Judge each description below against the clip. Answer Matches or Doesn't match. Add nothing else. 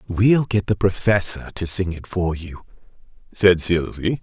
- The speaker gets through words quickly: Doesn't match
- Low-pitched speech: Matches